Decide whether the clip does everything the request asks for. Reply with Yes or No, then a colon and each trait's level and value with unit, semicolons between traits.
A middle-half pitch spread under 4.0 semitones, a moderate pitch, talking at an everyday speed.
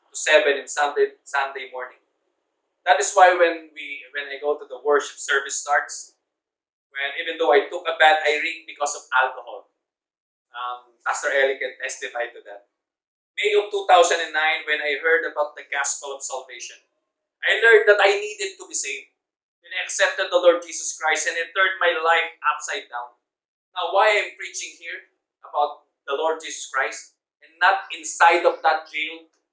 Yes: average, 3.5 semitones; medium, 160 Hz; average, 175 wpm